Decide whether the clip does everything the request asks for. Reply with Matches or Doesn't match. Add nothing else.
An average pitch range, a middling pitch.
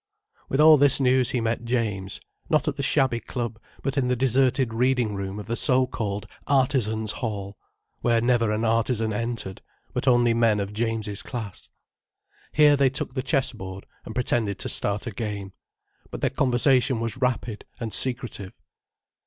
Doesn't match